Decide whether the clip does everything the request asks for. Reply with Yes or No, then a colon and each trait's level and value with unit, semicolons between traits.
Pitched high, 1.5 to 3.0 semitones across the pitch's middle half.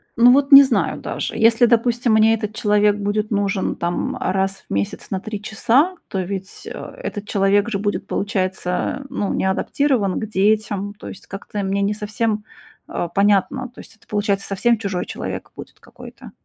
Yes: high, 205 Hz; narrow, 2.5 semitones